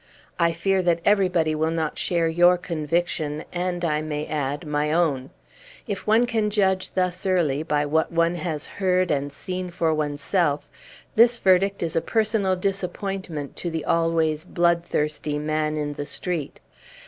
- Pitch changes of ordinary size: Yes, average, 3.3 semitones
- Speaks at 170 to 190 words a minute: No, average, 155 wpm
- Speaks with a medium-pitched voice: Yes, medium, 170 Hz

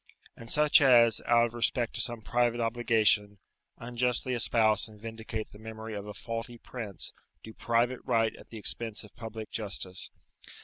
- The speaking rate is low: No, average, 165 wpm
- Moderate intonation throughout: No, narrow, 1.6 semitones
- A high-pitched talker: No, low, 115 Hz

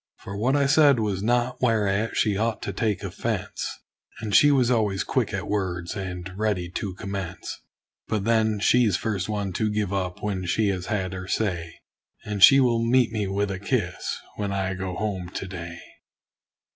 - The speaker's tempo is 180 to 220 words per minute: Yes, average, 185 wpm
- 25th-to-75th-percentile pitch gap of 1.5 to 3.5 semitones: Yes, average, 3.1 semitones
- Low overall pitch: Yes, low, 100 Hz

